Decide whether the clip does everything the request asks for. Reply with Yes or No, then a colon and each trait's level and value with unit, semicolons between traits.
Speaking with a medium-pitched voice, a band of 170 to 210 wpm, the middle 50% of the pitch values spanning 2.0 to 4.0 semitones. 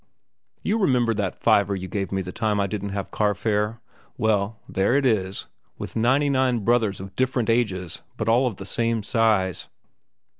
No: low, 110 Hz; average, 175 wpm; average, 3.3 semitones